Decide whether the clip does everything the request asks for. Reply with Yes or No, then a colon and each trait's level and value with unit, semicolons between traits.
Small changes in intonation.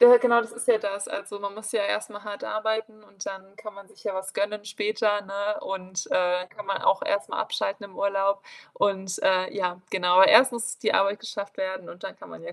Yes: narrow, 1.9 semitones